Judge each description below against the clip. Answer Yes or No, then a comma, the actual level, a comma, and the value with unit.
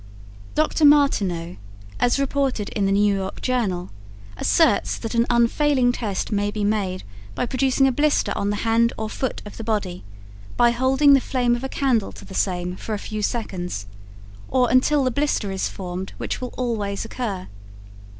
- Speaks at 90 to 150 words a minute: No, average, 175 wpm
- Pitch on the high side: Yes, high, 230 Hz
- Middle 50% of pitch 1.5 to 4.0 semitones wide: No, average, 4.5 semitones